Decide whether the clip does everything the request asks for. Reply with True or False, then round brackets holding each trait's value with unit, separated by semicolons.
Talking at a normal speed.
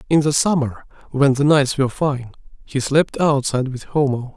True (180 wpm)